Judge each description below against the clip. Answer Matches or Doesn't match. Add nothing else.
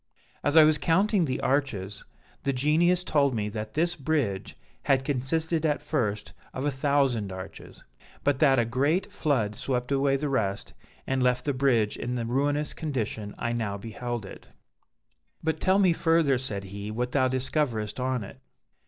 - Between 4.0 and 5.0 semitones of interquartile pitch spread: Matches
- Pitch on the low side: Matches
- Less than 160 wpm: Doesn't match